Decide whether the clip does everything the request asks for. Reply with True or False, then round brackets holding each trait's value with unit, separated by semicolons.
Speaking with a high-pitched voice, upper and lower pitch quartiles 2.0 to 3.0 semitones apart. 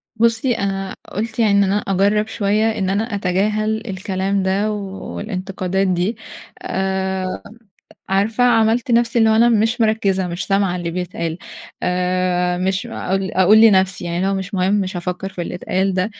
True (195 Hz; 2.6 semitones)